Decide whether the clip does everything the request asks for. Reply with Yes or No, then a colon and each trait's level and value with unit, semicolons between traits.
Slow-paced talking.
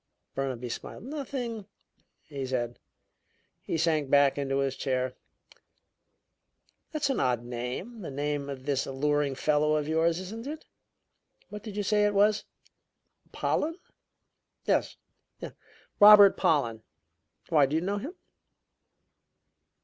Yes: slow, 120 wpm